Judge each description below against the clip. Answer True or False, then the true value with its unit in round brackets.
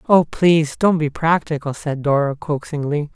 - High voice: False (150 Hz)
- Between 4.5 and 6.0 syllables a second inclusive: True (5.0 syllables/s)